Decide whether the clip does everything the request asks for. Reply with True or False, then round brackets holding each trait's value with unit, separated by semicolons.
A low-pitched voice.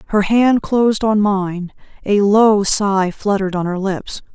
False (205 Hz)